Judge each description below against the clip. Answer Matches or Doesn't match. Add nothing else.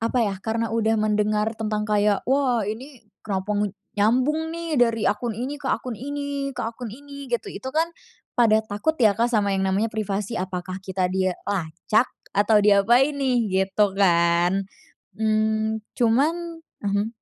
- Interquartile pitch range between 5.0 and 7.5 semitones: Doesn't match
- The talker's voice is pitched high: Matches